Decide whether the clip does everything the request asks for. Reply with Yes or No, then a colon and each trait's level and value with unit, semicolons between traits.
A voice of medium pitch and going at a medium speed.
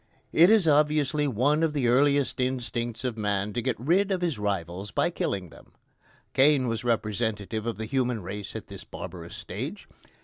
No: low, 120 Hz; average, 175 wpm